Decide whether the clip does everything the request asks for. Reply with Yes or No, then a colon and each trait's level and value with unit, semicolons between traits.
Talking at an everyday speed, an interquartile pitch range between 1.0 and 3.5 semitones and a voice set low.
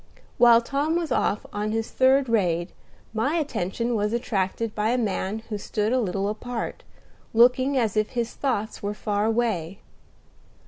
No: average, 155 wpm; average, 3.1 semitones; high, 225 Hz